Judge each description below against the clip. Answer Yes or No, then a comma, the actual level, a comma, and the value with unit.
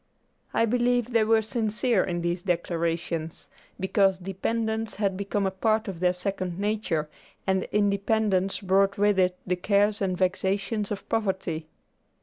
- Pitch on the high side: Yes, high, 195 Hz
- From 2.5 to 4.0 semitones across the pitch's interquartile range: Yes, average, 2.9 semitones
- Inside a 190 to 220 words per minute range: No, average, 140 wpm